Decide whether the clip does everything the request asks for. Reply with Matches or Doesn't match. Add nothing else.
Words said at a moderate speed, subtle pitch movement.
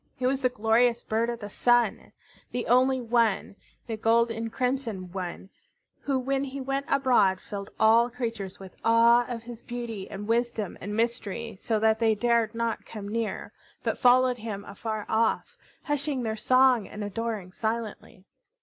Matches